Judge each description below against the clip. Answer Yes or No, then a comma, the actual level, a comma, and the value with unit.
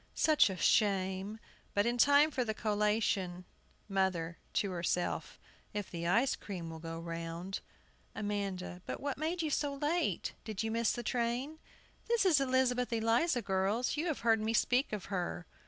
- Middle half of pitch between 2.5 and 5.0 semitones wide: No, wide, 5.4 semitones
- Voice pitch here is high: Yes, high, 215 Hz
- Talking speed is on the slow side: No, average, 170 wpm